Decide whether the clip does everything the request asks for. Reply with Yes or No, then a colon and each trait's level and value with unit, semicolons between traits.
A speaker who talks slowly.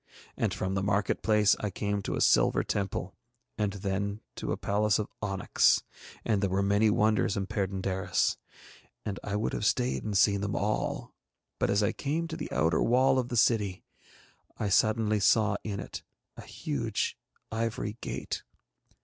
No: average, 170 wpm